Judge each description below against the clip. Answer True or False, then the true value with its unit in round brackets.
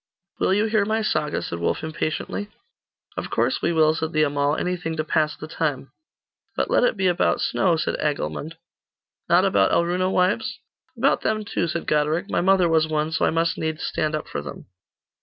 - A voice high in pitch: False (160 Hz)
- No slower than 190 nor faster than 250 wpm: True (195 wpm)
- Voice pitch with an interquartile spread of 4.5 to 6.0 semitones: False (3.2 semitones)